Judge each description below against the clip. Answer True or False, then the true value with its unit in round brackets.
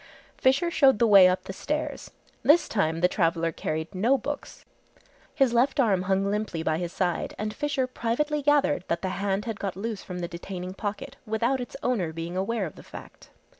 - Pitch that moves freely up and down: True (5.9 semitones)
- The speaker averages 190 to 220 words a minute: True (195 wpm)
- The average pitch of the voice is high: True (205 Hz)